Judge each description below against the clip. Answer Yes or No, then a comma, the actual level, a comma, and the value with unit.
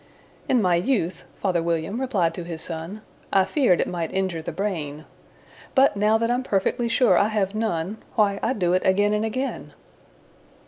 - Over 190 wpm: No, average, 180 wpm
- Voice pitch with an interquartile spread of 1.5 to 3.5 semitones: No, average, 4.3 semitones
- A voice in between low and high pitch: No, high, 195 Hz